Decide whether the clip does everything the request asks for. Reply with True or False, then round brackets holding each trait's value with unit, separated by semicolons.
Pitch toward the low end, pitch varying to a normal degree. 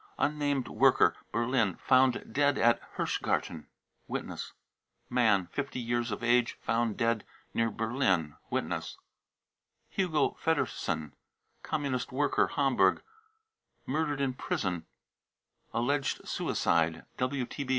True (120 Hz; 4.3 semitones)